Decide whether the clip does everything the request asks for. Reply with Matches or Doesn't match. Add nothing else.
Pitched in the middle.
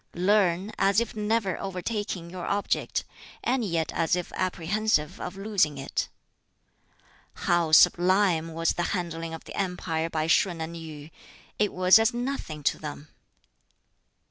Matches